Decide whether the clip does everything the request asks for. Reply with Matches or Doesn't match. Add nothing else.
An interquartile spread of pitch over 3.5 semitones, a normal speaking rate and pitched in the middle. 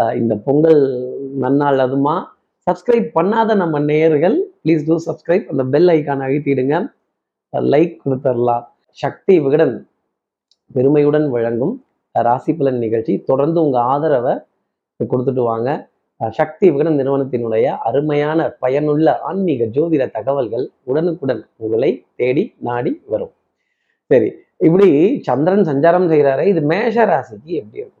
Matches